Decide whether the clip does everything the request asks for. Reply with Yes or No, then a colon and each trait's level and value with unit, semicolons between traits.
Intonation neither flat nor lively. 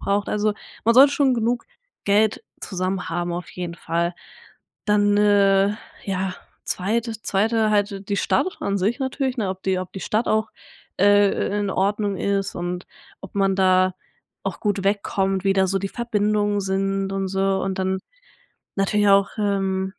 No: narrow, 1.5 semitones